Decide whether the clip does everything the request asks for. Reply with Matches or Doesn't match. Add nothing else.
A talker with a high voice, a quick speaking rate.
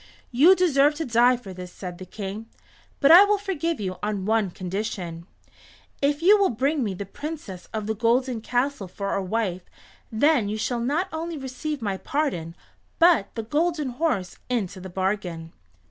Doesn't match